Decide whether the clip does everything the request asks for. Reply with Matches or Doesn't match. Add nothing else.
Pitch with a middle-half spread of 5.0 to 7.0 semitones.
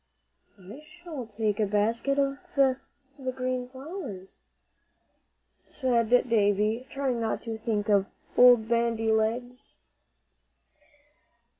Doesn't match